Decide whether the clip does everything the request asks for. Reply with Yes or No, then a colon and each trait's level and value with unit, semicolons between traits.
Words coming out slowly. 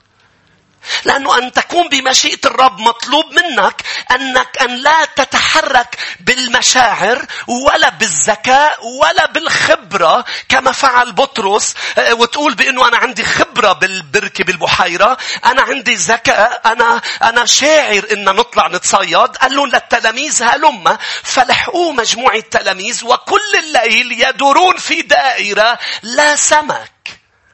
Yes: slow, 105 wpm